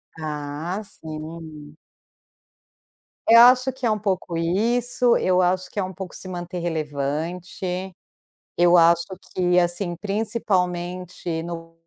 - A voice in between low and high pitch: Yes, medium, 180 Hz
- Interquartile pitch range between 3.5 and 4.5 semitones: No, narrow, 2.6 semitones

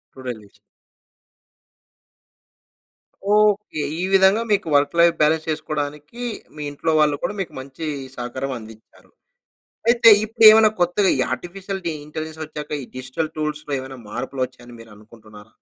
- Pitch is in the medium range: Yes, medium, 150 Hz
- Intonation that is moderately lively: No, wide, 5.8 semitones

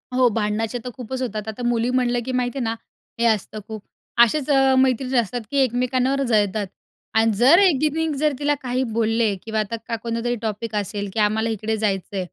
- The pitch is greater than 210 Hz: Yes, high, 235 Hz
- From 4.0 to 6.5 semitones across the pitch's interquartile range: No, average, 2.9 semitones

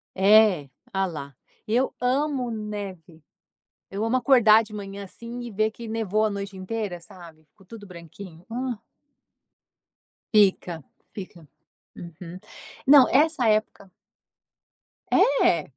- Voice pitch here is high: Yes, high, 210 Hz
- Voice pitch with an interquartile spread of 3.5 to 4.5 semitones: Yes, average, 4.0 semitones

